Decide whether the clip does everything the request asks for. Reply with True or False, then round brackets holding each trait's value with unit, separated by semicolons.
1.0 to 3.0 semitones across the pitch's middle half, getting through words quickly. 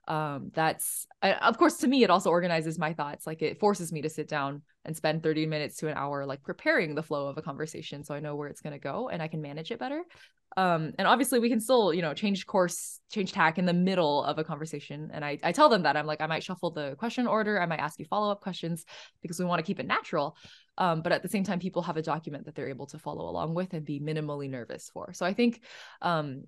False (4.2 semitones; 265 wpm)